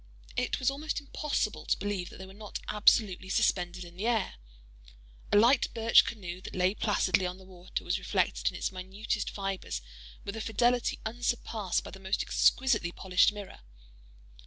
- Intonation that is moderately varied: Yes, average, 3.5 semitones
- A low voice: No, high, 205 Hz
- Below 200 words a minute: Yes, average, 170 wpm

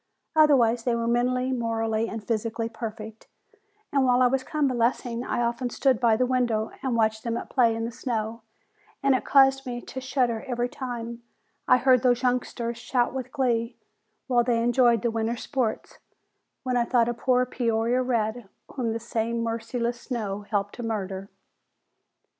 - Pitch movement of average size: No, narrow, 1.9 semitones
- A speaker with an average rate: Yes, average, 170 wpm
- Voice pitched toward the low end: No, high, 235 Hz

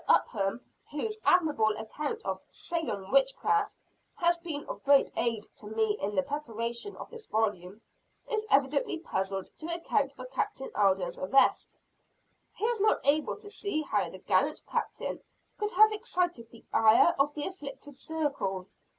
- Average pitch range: No, wide, 7.7 semitones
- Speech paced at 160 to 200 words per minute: No, average, 150 wpm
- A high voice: Yes, very high, 280 Hz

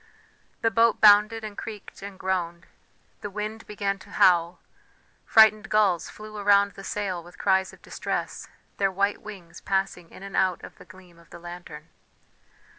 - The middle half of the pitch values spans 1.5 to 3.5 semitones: Yes, average, 2.8 semitones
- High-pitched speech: Yes, high, 195 Hz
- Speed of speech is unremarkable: Yes, average, 165 wpm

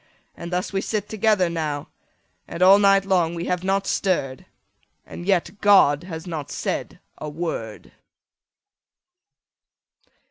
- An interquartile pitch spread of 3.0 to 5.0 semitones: Yes, average, 3.3 semitones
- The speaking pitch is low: No, medium, 180 Hz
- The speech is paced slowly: Yes, slow, 130 wpm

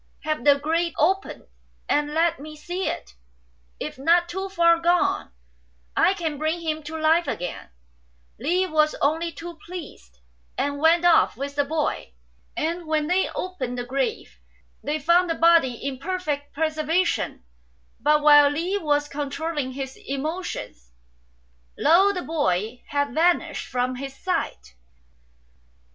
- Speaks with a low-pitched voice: No, very high, 310 Hz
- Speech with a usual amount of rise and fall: Yes, average, 3.3 semitones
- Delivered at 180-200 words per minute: No, average, 140 wpm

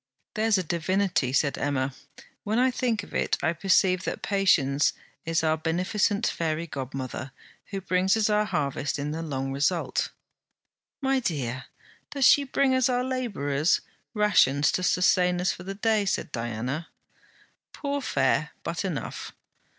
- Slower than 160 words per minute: Yes, average, 150 wpm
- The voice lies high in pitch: No, medium, 180 Hz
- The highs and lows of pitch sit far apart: Yes, wide, 6.6 semitones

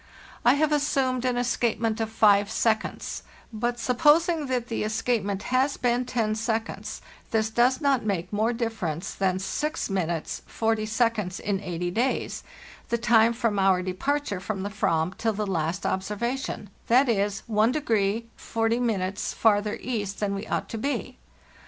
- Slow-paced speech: No, average, 145 wpm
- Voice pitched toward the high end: Yes, high, 220 Hz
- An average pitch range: Yes, average, 3.5 semitones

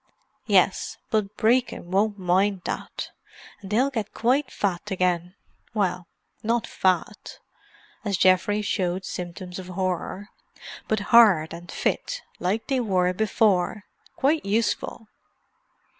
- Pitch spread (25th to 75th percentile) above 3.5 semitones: No, average, 3.2 semitones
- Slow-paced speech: Yes, slow, 115 wpm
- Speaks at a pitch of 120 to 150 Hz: No, high, 200 Hz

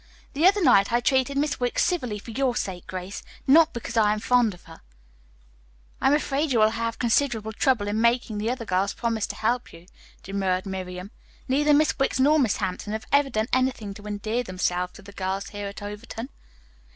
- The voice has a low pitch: No, high, 225 Hz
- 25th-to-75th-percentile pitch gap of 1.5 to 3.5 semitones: No, average, 4.5 semitones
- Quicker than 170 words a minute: Yes, average, 200 wpm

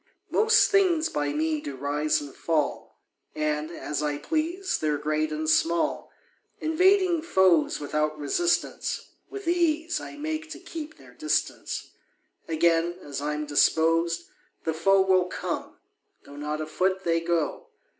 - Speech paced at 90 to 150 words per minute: Yes, average, 140 wpm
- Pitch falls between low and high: Yes, medium, 165 Hz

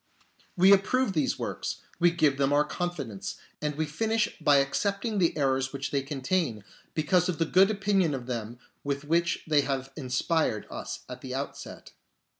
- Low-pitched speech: No, medium, 150 Hz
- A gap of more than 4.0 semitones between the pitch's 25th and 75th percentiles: Yes, average, 5.0 semitones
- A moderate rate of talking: Yes, average, 170 wpm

